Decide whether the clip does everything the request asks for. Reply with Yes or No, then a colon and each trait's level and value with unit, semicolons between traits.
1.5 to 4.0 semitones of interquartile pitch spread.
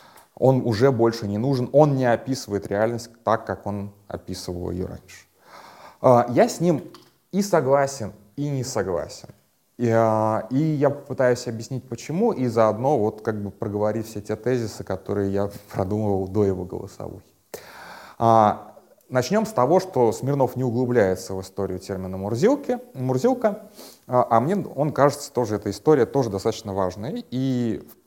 No: average, 4.7 semitones